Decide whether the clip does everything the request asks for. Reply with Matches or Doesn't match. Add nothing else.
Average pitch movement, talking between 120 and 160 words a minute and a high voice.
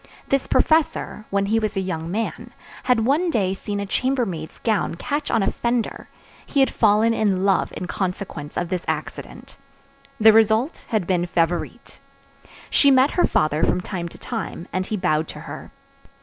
Doesn't match